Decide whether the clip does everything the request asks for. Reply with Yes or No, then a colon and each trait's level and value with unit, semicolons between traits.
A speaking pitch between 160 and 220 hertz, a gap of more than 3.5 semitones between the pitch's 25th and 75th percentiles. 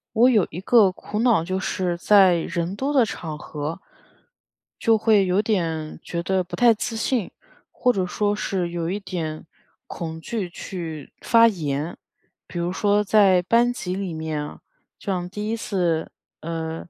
Yes: medium, 185 Hz; average, 4.0 semitones